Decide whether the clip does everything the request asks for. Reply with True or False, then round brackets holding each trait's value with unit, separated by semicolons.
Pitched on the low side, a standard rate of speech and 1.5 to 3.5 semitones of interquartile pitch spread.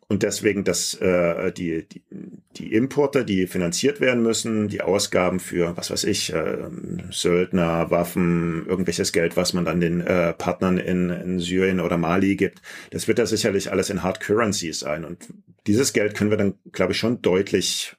True (90 Hz; 180 wpm; 2.9 semitones)